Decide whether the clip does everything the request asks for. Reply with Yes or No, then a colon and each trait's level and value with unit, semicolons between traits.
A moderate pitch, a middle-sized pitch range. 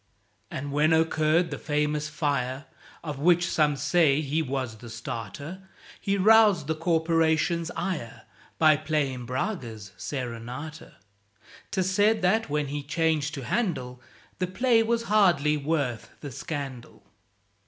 Yes: medium, 155 Hz; average, 4.1 semitones